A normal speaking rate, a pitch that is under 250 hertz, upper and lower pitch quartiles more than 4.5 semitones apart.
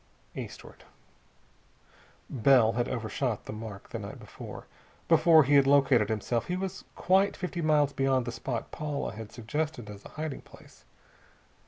Yes: average, 150 wpm; low, 135 Hz; average, 5.2 semitones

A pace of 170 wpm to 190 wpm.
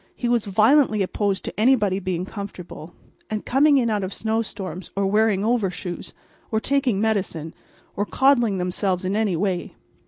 No: average, 160 wpm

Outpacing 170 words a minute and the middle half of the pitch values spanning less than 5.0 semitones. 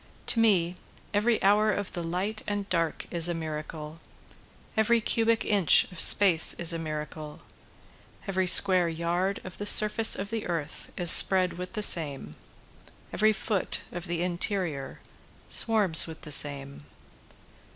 No: average, 145 wpm; average, 4.0 semitones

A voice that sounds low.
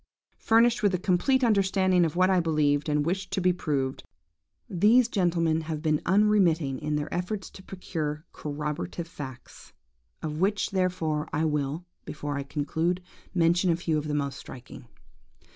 No: medium, 165 Hz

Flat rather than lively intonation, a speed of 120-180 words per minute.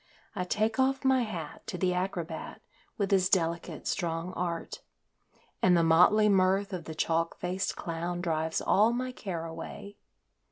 No: average, 3.3 semitones; average, 155 wpm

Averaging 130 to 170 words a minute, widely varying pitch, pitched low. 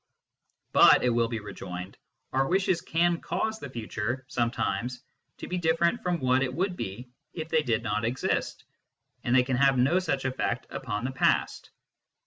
No: average, 180 wpm; wide, 5.9 semitones; low, 130 Hz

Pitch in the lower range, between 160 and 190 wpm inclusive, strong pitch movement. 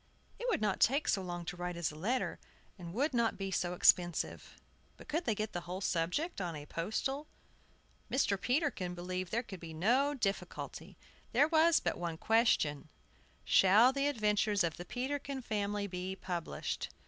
No: high, 200 Hz; average, 170 wpm; wide, 6.4 semitones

